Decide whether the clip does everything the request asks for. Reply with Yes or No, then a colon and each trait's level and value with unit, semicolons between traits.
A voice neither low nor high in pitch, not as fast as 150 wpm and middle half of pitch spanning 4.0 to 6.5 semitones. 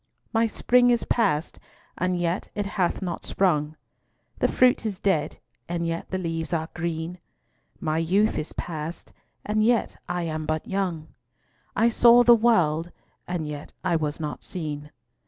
No: medium, 175 Hz; average, 155 wpm; average, 4.5 semitones